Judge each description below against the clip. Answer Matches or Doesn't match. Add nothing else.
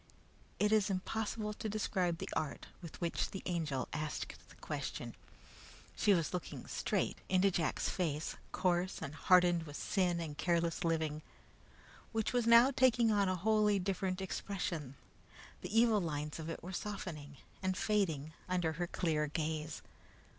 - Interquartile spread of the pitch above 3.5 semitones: Matches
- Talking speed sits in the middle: Matches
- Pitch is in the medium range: Matches